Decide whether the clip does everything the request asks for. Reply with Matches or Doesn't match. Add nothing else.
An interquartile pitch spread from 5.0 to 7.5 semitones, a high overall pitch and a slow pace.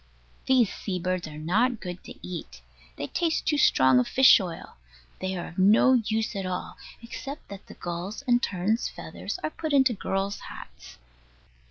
Doesn't match